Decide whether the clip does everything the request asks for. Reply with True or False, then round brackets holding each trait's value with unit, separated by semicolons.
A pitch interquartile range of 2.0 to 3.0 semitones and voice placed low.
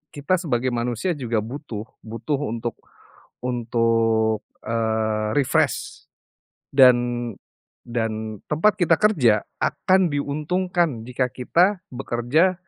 False (5.0 semitones; 125 Hz)